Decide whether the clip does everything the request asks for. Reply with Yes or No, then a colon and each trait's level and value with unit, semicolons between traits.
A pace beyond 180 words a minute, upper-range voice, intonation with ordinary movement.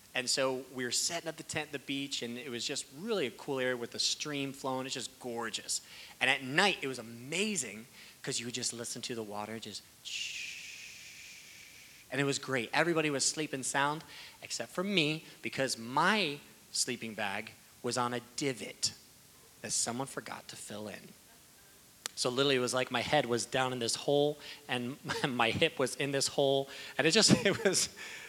No: average, 190 wpm; low, 135 Hz; average, 3.6 semitones